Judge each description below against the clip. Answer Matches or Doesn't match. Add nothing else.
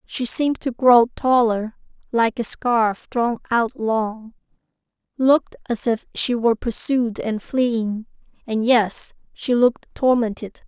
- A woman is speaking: Matches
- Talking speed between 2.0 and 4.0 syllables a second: Matches